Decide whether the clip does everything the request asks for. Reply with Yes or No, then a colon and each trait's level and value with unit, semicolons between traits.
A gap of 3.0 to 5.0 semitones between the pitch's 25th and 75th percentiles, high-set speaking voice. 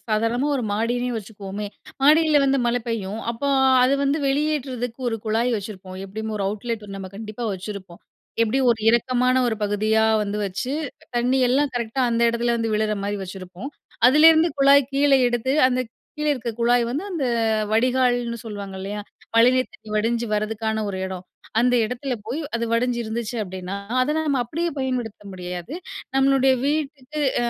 Yes: average, 3.7 semitones; high, 235 Hz